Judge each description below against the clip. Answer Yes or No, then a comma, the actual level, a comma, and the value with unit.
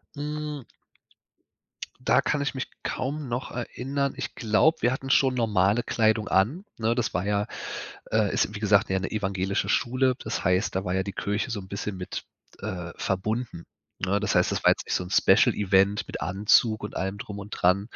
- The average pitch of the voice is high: No, low, 105 Hz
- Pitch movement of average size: Yes, average, 4.5 semitones